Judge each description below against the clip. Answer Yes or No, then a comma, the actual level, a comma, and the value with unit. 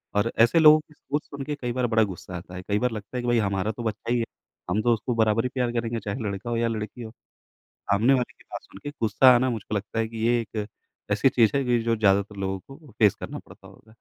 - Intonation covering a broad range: No, average, 2.9 semitones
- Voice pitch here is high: No, low, 115 Hz